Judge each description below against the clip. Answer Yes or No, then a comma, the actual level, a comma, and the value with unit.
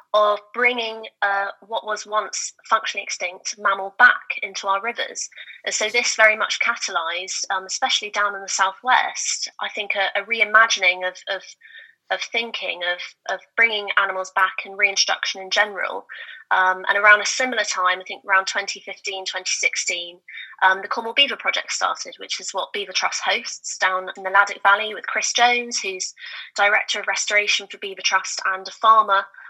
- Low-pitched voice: No, high, 200 Hz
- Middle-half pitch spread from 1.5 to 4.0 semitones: Yes, average, 2.7 semitones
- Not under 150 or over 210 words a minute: Yes, average, 170 wpm